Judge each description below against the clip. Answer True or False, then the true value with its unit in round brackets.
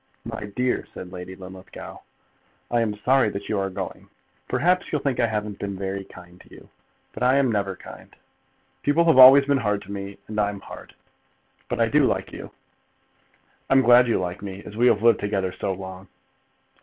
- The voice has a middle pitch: False (105 Hz)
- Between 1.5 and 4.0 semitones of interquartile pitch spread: False (4.4 semitones)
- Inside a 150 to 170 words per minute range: False (195 wpm)